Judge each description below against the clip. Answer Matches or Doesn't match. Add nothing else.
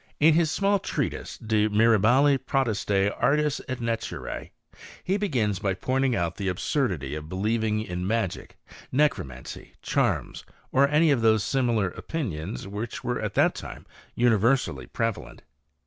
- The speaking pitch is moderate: Doesn't match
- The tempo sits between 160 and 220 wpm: Doesn't match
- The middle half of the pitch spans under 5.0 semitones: Doesn't match